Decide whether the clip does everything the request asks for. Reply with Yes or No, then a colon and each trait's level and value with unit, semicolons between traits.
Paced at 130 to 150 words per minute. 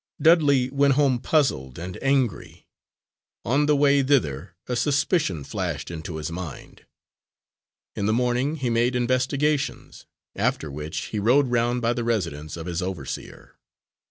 Yes: average, 140 wpm